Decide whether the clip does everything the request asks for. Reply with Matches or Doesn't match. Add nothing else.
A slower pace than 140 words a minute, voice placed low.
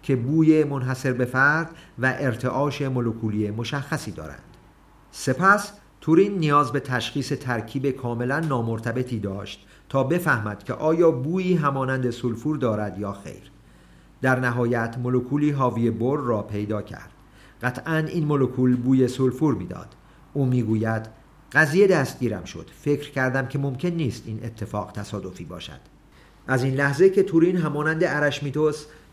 Matches